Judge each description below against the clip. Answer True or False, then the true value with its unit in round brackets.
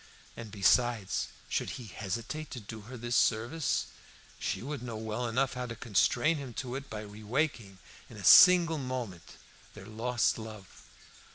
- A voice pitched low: True (120 Hz)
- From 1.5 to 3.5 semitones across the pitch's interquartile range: True (3.2 semitones)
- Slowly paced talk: False (165 wpm)